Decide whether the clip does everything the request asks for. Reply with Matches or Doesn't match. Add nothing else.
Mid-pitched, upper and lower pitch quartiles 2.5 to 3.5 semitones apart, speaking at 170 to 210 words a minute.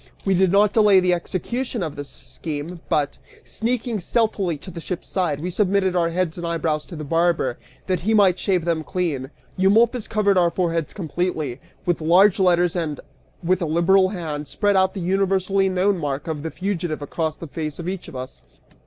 Matches